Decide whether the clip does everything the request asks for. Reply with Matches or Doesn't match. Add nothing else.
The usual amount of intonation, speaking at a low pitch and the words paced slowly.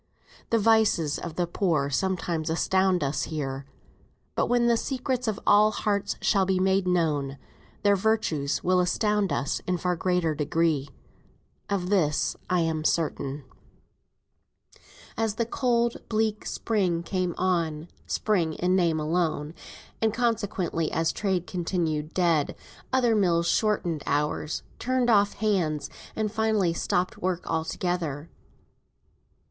Doesn't match